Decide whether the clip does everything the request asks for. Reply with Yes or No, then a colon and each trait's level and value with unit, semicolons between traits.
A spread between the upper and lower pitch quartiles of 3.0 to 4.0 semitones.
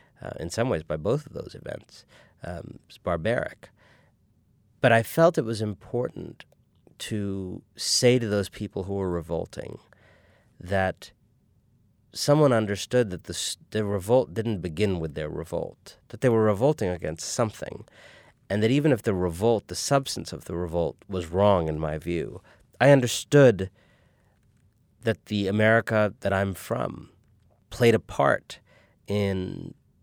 Yes: average, 3.5 semitones